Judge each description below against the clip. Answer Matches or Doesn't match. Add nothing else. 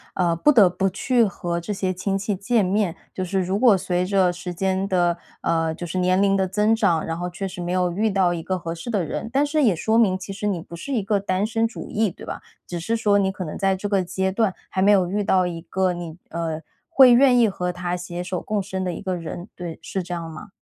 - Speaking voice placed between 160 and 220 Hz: Matches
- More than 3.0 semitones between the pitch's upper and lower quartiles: Doesn't match